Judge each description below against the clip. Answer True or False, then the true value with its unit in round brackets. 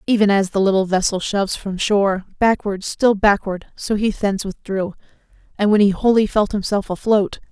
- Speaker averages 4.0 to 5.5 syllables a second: True (5.2 syllables/s)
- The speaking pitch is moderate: False (200 Hz)